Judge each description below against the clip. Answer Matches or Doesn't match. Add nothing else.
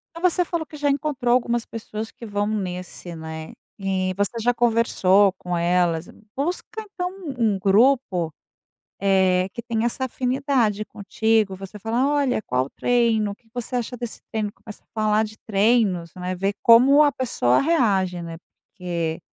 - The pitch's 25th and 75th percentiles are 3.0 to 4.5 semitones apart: Doesn't match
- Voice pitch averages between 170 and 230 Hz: Matches